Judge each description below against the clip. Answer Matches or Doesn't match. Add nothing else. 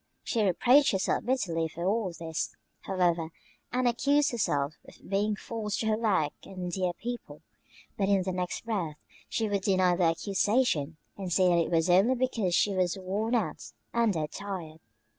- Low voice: Doesn't match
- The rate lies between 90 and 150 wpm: Doesn't match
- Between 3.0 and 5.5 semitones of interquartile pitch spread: Matches